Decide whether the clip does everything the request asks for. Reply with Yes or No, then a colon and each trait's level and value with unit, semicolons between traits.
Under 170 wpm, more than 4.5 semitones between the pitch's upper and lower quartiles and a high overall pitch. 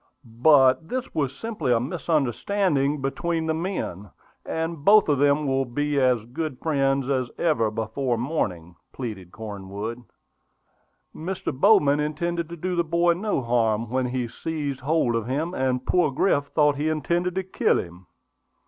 No: average, 155 wpm; average, 5.1 semitones; medium, 140 Hz